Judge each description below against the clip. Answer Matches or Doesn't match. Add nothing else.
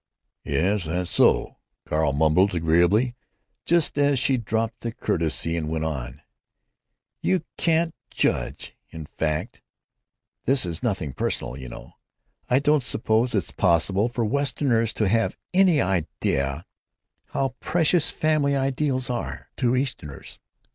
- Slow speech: Matches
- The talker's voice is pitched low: Matches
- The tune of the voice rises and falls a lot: Matches